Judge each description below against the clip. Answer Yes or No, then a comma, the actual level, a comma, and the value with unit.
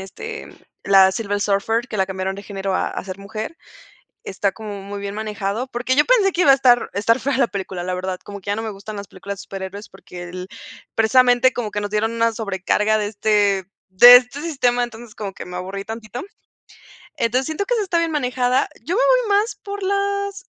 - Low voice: No, high, 220 Hz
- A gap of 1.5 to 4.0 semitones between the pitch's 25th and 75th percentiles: No, average, 4.6 semitones